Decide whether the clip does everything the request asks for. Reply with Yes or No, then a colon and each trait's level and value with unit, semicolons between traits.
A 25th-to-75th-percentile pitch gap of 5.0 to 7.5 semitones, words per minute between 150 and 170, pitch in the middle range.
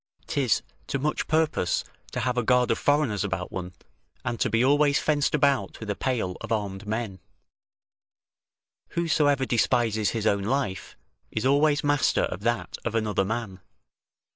No: average, 5.3 semitones; average, 155 wpm; low, 120 Hz